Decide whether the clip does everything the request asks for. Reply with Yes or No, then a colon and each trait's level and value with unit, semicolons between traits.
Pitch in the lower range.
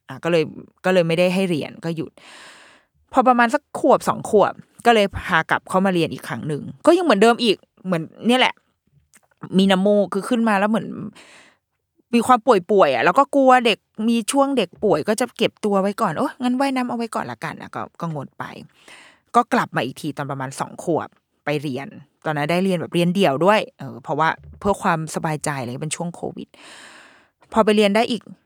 No: high, 200 Hz